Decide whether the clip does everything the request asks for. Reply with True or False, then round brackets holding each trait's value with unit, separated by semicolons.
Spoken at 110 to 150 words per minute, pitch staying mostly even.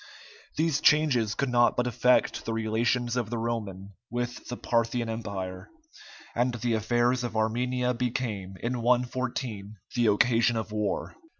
True (140 wpm; 2.1 semitones)